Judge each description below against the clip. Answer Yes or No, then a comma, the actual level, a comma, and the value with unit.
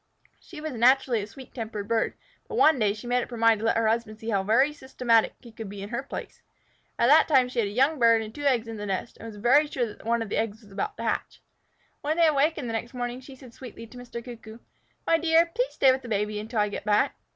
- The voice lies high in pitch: Yes, high, 235 Hz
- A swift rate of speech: Yes, fast, 270 wpm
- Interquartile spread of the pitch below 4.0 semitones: Yes, average, 3.4 semitones